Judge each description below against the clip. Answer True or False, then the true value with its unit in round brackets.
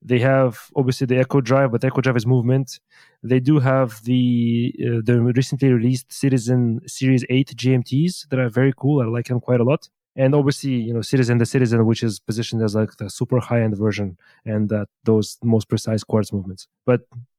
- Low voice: True (125 Hz)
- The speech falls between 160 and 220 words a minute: True (200 wpm)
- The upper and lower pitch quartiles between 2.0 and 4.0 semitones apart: True (2.5 semitones)